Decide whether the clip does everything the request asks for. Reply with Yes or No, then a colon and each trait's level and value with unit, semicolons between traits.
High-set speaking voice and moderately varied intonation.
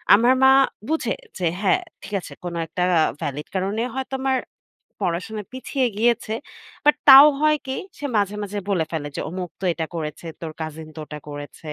No: high, 200 Hz; wide, 8.2 semitones